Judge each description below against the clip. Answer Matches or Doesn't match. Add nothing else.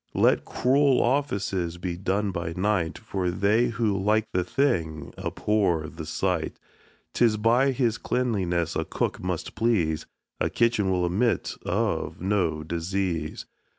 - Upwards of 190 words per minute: Doesn't match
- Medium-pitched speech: Doesn't match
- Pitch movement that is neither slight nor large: Matches